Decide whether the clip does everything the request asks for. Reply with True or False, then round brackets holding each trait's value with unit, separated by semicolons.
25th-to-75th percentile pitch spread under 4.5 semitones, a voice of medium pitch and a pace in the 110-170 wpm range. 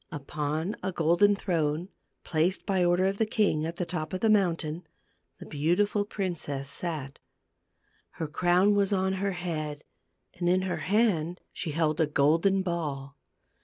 True (3.6 semitones; 175 Hz; 155 wpm)